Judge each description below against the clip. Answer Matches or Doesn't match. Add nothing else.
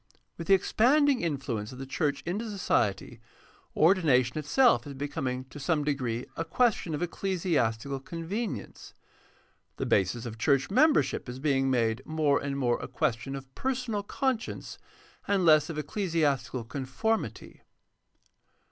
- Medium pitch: Matches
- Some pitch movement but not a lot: Doesn't match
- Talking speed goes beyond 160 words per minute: Doesn't match